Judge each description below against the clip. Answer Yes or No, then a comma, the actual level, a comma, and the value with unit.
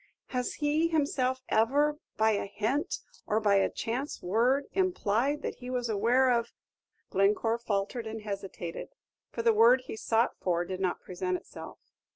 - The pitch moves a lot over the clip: No, average, 4.3 semitones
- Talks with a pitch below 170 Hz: No, high, 230 Hz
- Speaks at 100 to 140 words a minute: No, average, 165 wpm